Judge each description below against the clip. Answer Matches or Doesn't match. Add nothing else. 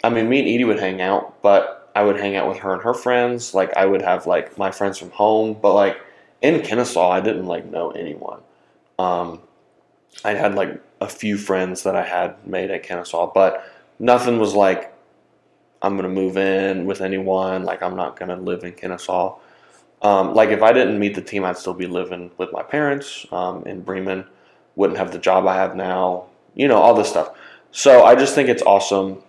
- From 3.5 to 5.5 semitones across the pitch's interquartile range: Doesn't match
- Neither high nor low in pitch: Doesn't match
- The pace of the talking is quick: Matches